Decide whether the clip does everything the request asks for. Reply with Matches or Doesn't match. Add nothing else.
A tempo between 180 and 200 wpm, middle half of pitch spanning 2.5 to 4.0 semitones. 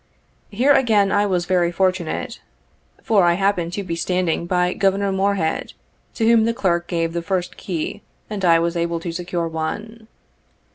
Doesn't match